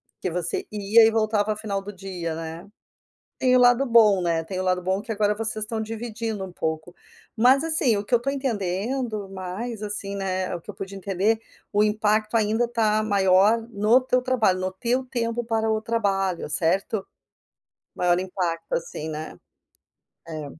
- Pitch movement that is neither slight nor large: Yes, average, 3.5 semitones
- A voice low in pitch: No, high, 210 Hz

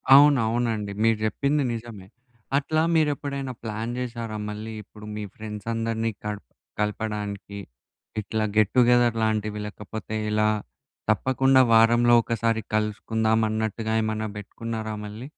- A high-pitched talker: No, low, 110 Hz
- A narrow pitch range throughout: Yes, narrow, 1.8 semitones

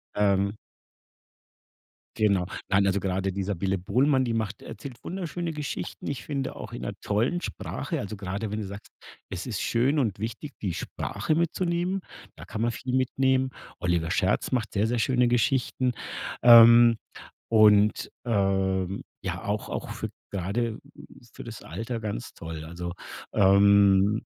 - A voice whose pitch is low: Yes, low, 110 Hz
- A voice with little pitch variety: No, average, 4.4 semitones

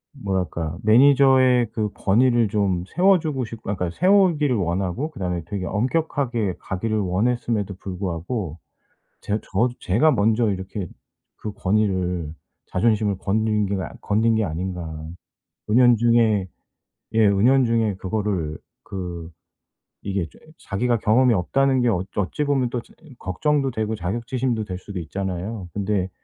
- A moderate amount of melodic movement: Yes, average, 4.5 semitones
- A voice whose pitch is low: Yes, low, 105 Hz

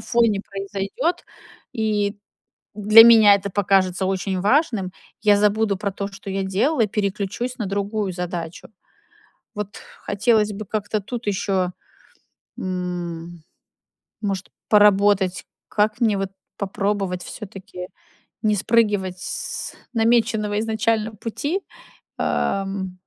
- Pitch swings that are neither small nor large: No, narrow, 2.2 semitones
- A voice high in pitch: Yes, high, 205 Hz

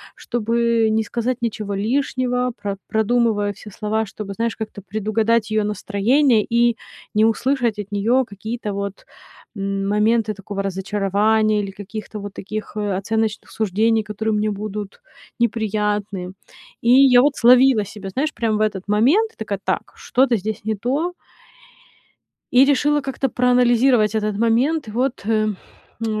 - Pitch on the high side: Yes, high, 220 Hz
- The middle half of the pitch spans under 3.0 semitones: Yes, narrow, 2.6 semitones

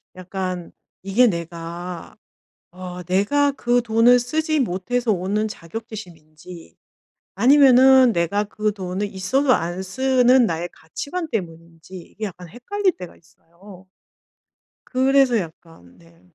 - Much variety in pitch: Yes, wide, 6.2 semitones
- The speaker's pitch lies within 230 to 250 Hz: No, high, 195 Hz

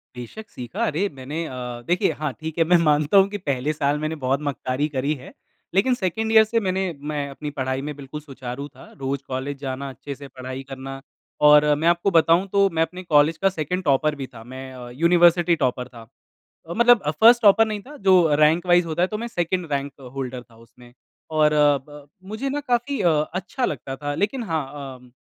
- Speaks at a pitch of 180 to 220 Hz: No, medium, 150 Hz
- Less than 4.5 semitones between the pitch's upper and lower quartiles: No, average, 5.3 semitones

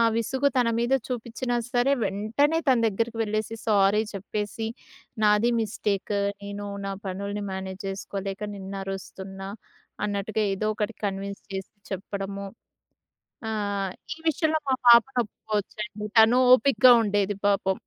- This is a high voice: Yes, high, 210 Hz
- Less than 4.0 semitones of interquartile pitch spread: Yes, average, 2.8 semitones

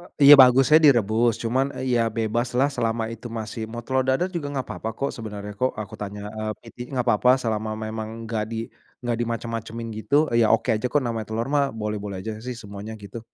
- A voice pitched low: Yes, low, 115 Hz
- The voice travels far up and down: No, narrow, 2.5 semitones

